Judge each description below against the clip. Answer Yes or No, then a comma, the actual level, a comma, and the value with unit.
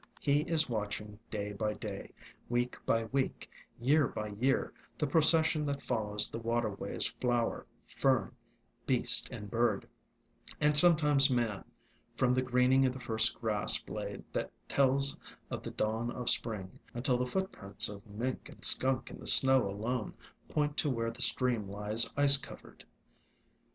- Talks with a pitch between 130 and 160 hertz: No, low, 120 Hz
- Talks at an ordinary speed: Yes, average, 155 wpm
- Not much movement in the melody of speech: No, average, 3.8 semitones